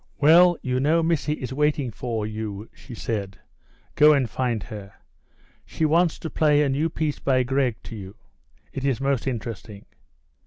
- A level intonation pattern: No, average, 5.1 semitones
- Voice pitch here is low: Yes, low, 130 Hz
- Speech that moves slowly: No, average, 165 wpm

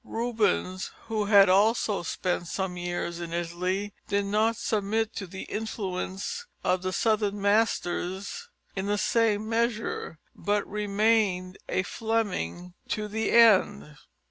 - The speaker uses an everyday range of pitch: Yes, average, 3.2 semitones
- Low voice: No, high, 200 Hz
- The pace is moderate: No, slow, 125 wpm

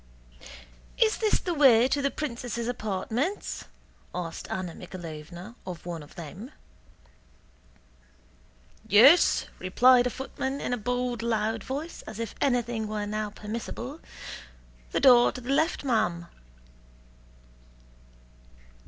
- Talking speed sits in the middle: No, slow, 115 wpm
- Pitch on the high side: Yes, high, 235 Hz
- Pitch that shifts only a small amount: No, average, 4.3 semitones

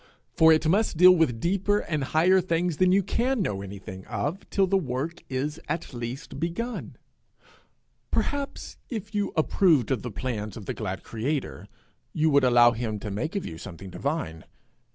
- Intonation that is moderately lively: No, wide, 7.9 semitones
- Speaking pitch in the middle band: Yes, medium, 150 Hz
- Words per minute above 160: Yes, average, 175 wpm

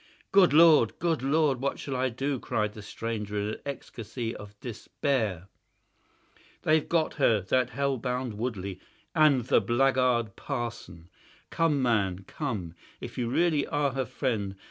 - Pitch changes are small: No, average, 4.7 semitones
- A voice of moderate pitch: No, low, 125 Hz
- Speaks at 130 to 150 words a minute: Yes, average, 145 wpm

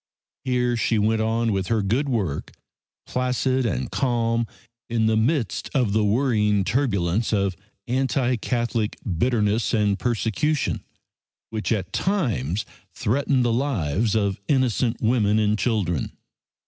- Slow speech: Yes, slow, 125 wpm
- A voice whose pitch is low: Yes, low, 115 Hz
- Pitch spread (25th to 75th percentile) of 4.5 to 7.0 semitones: No, average, 3.3 semitones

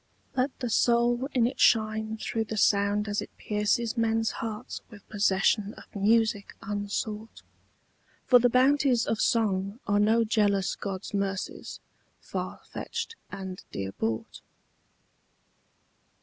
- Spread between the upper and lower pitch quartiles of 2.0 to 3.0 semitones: Yes, narrow, 2.4 semitones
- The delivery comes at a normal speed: No, slow, 125 wpm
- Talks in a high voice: Yes, high, 215 Hz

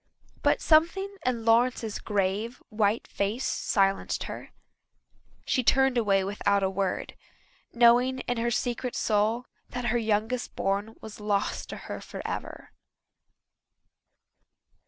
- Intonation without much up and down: No, average, 3.4 semitones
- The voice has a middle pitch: No, high, 225 Hz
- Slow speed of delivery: Yes, slow, 115 wpm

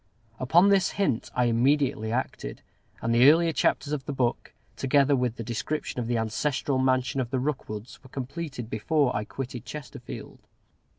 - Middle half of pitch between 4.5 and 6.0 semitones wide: No, average, 3.5 semitones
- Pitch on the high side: No, low, 130 Hz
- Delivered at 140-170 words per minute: Yes, average, 165 wpm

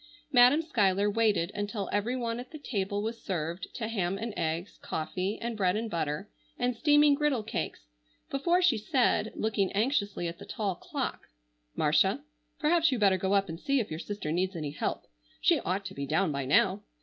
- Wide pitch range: No, average, 4.7 semitones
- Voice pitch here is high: Yes, high, 205 Hz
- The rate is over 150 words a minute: Yes, average, 190 wpm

